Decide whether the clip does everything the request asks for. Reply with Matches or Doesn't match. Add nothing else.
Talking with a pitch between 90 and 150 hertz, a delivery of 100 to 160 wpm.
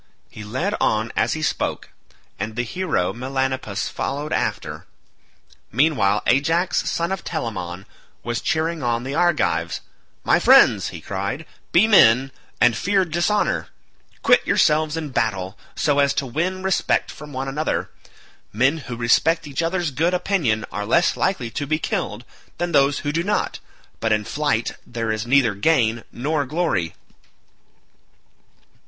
Matches